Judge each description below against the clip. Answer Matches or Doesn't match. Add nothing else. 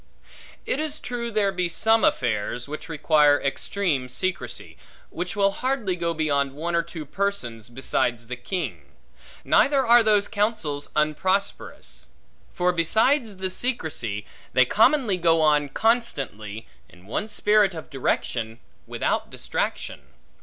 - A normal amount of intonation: Doesn't match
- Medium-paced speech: Doesn't match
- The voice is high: Doesn't match